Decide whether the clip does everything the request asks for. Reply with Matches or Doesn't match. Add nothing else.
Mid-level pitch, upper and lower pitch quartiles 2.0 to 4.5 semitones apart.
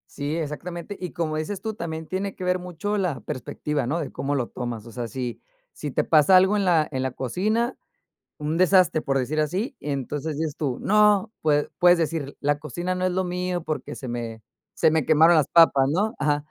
Matches